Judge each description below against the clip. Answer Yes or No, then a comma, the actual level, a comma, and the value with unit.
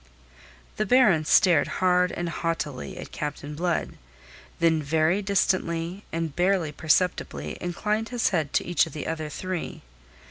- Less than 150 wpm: Yes, average, 140 wpm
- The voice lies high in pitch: No, medium, 170 Hz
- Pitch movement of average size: Yes, average, 3.0 semitones